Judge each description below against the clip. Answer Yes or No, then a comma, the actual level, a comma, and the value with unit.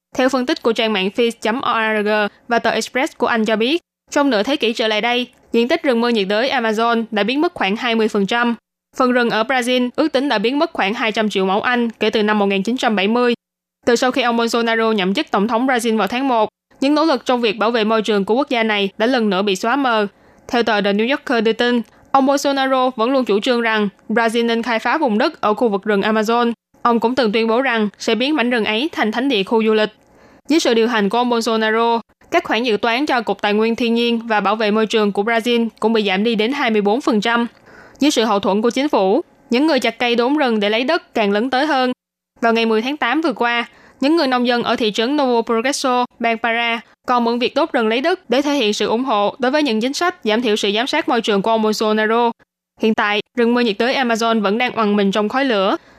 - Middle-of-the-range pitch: No, high, 235 Hz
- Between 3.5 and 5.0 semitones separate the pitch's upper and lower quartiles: No, narrow, 2.6 semitones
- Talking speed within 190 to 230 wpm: No, fast, 250 wpm